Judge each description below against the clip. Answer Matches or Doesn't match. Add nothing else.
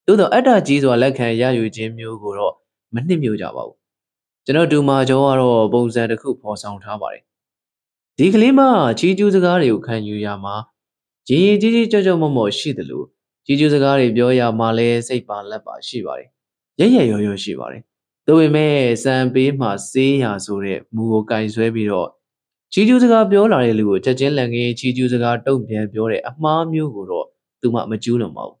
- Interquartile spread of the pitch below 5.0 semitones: Doesn't match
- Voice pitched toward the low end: Matches